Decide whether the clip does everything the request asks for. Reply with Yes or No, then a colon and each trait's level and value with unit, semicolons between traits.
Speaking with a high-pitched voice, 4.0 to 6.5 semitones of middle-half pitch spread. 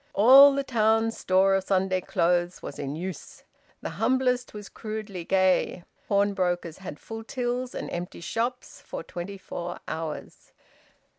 Yes: high, 195 Hz; average, 4.5 semitones